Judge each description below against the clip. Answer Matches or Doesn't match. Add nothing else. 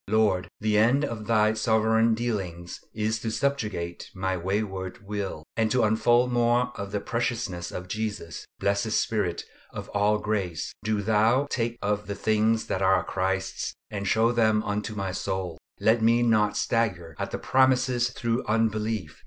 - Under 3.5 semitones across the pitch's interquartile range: Matches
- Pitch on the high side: Doesn't match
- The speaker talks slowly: Doesn't match